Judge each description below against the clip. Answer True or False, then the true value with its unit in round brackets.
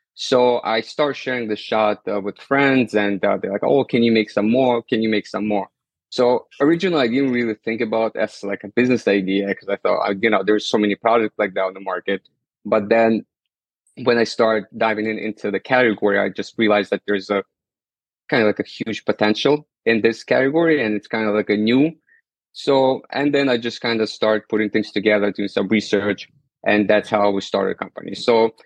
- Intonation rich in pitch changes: False (2.9 semitones)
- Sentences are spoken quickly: True (220 wpm)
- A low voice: True (110 Hz)